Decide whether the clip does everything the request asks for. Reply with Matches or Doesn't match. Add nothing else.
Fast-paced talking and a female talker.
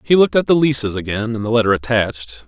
Doesn't match